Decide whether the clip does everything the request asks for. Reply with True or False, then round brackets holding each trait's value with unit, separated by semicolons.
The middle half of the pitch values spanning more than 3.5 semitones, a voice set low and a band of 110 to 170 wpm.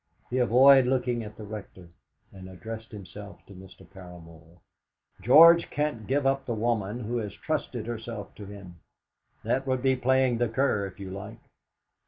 True (4.7 semitones; 110 Hz; 165 wpm)